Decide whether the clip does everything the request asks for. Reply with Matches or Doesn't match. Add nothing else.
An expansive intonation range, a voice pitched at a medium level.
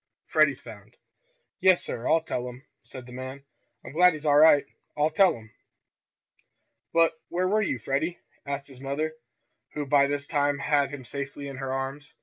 Doesn't match